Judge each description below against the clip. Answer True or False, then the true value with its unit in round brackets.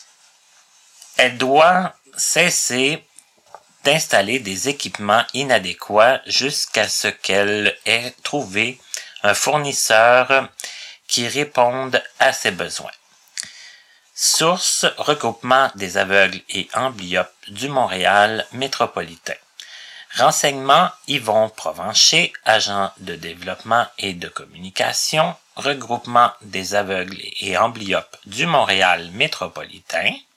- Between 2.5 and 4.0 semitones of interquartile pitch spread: False (4.9 semitones)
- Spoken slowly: True (90 wpm)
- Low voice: True (120 Hz)